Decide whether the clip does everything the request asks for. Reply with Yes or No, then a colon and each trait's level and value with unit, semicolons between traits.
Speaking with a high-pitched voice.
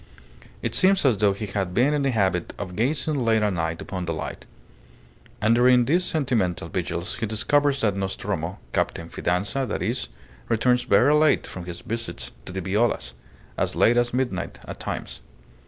No: low, 110 Hz